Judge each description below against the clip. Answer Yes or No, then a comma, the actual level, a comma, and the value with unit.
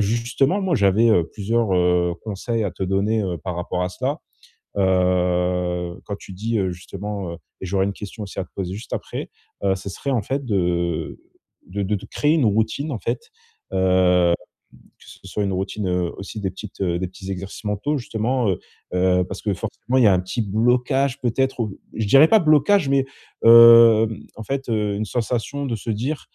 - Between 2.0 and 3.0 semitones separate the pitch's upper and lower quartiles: No, average, 4.2 semitones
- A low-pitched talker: Yes, low, 100 Hz